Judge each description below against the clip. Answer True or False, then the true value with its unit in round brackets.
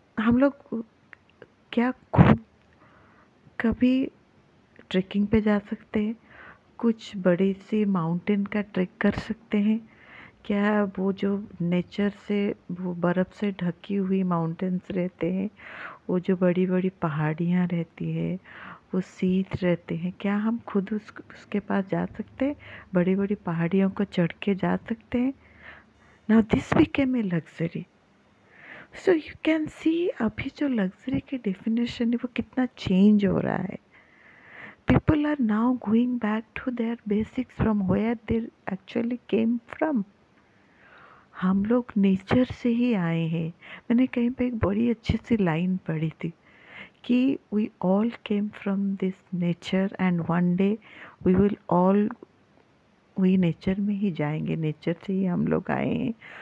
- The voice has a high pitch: True (205 Hz)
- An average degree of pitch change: True (4.0 semitones)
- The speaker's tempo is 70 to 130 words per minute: False (145 wpm)